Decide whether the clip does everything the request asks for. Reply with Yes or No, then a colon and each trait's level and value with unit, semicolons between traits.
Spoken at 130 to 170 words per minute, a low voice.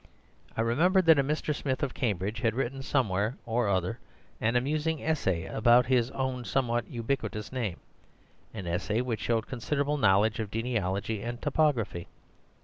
Yes: average, 150 wpm; low, 120 Hz